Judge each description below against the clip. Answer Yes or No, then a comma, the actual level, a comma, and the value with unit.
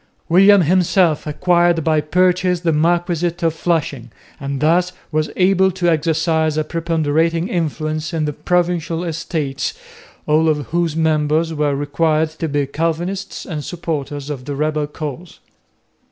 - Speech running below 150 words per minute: Yes, average, 140 wpm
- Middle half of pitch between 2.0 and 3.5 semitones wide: Yes, narrow, 2.4 semitones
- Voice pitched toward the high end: No, medium, 160 Hz